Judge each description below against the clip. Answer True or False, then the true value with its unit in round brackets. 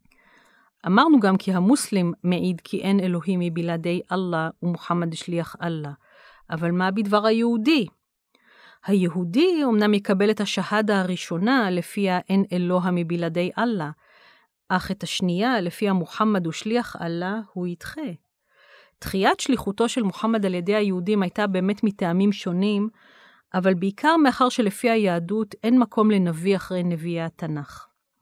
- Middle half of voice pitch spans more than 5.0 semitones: False (3.7 semitones)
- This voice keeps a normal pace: True (130 wpm)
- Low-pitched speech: False (190 Hz)